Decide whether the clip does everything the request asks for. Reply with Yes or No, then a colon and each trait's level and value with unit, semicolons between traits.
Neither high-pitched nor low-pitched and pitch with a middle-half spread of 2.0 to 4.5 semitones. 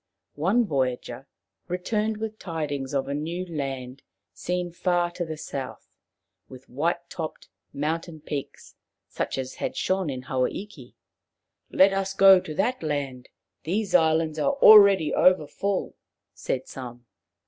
No: medium, 160 Hz; average, 5.2 semitones